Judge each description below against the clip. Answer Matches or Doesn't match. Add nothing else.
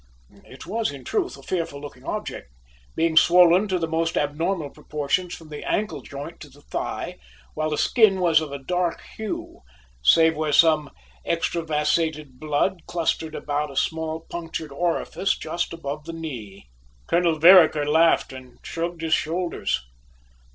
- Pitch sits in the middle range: Matches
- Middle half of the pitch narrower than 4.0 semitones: Matches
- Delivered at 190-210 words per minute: Doesn't match